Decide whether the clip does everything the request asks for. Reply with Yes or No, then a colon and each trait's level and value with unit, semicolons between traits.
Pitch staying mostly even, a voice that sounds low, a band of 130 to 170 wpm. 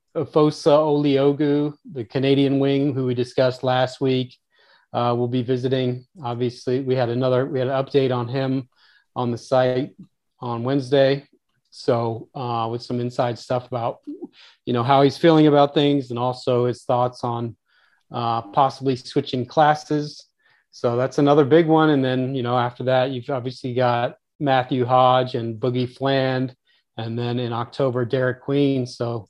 Yes: narrow, 2.1 semitones; low, 130 Hz; average, 160 wpm